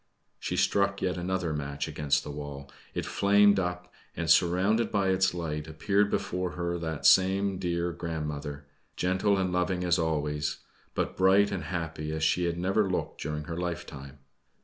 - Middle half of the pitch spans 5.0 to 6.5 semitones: No, average, 3.6 semitones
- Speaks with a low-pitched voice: Yes, very low, 85 Hz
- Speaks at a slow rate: No, average, 165 wpm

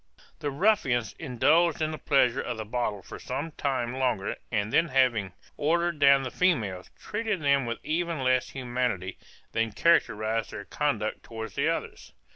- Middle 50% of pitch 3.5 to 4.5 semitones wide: No, wide, 5.4 semitones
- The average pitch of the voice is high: No, low, 130 Hz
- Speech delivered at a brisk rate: No, average, 160 wpm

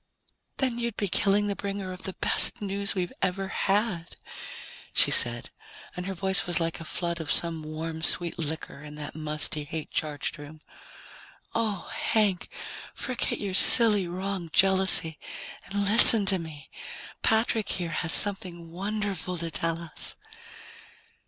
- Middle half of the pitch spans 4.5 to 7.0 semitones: No, average, 3.5 semitones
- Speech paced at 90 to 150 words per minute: Yes, average, 145 wpm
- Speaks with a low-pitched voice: No, medium, 185 Hz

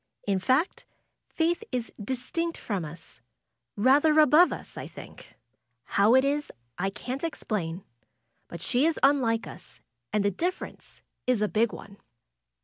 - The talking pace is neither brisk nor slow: Yes, average, 145 wpm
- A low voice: No, very high, 250 Hz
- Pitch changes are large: Yes, wide, 6.8 semitones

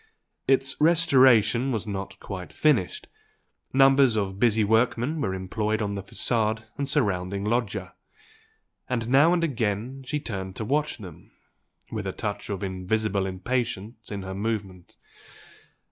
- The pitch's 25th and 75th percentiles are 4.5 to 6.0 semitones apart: Yes, average, 4.8 semitones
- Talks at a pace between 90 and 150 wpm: Yes, slow, 135 wpm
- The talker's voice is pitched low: Yes, low, 110 Hz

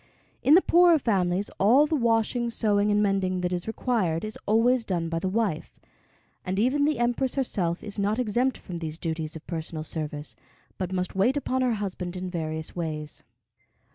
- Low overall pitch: No, high, 200 Hz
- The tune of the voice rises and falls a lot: Yes, wide, 5.8 semitones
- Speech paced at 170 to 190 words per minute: Yes, average, 180 wpm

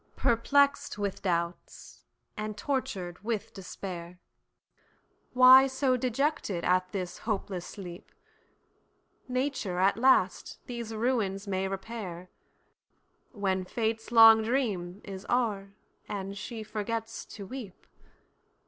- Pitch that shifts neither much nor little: Yes, average, 4.1 semitones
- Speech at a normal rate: No, slow, 95 wpm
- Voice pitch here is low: No, high, 210 Hz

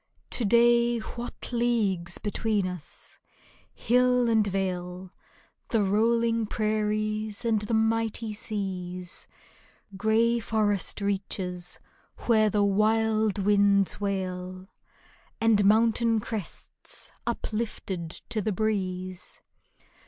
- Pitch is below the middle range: No, high, 215 Hz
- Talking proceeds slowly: Yes, slow, 95 wpm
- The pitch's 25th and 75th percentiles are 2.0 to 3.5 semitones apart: Yes, average, 2.8 semitones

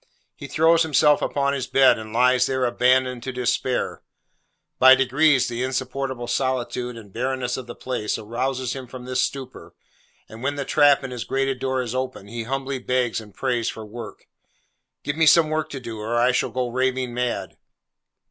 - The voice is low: Yes, low, 130 Hz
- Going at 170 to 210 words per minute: Yes, average, 185 wpm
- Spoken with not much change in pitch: Yes, narrow, 1.9 semitones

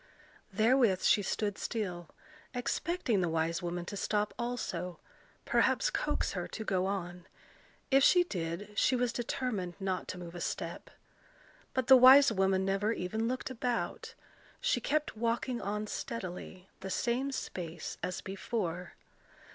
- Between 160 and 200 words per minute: No, average, 140 wpm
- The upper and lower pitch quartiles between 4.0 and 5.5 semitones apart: Yes, average, 5.1 semitones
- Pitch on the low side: No, high, 205 Hz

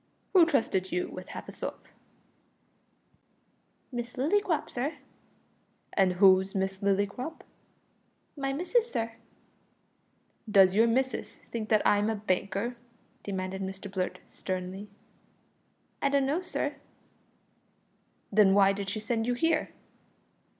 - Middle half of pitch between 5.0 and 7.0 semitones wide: Yes, wide, 5.5 semitones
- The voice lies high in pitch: Yes, high, 210 Hz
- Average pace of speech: No, slow, 115 wpm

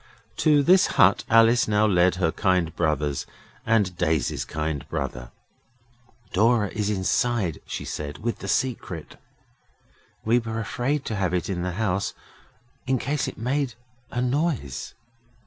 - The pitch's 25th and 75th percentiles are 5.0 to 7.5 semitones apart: Yes, wide, 5.6 semitones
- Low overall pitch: Yes, low, 105 Hz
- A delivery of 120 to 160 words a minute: Yes, average, 140 wpm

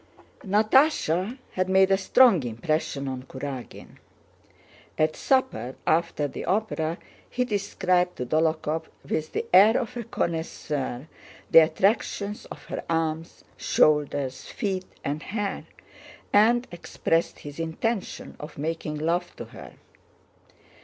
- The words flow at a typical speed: No, slow, 120 wpm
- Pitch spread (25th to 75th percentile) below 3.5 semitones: No, average, 4.9 semitones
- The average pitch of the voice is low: No, medium, 165 Hz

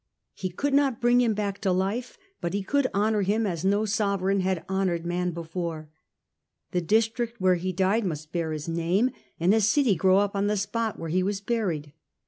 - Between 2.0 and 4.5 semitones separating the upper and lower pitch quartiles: Yes, average, 3.8 semitones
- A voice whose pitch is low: No, high, 195 Hz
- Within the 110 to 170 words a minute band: No, average, 195 wpm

